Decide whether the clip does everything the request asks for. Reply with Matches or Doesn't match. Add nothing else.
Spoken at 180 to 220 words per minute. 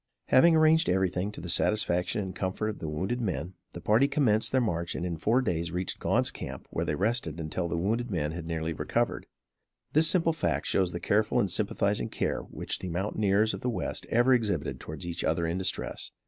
Matches